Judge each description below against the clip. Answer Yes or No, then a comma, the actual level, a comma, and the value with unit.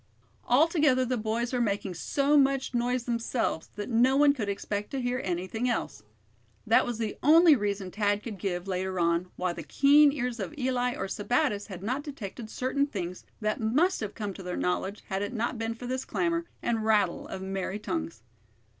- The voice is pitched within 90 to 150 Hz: No, high, 225 Hz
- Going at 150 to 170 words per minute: No, average, 190 wpm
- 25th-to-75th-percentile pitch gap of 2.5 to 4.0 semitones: No, average, 4.7 semitones